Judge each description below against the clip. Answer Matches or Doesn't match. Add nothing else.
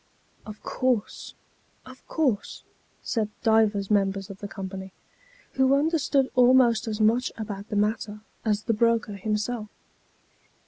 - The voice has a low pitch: Doesn't match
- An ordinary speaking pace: Doesn't match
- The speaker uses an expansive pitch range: Doesn't match